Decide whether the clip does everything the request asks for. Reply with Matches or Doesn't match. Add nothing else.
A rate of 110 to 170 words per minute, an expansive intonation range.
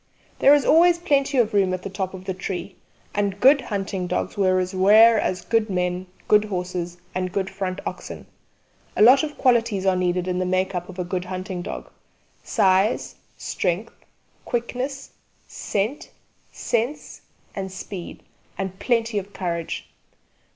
Doesn't match